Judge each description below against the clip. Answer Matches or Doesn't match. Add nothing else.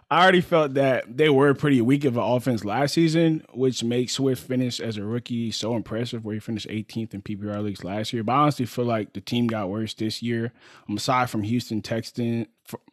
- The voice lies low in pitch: Matches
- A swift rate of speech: Matches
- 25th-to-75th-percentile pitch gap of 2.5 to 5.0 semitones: Matches